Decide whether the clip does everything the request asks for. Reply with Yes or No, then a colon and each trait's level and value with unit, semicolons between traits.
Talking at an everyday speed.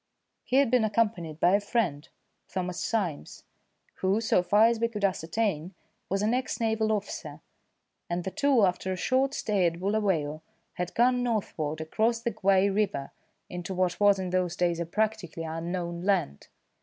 Yes: average, 170 wpm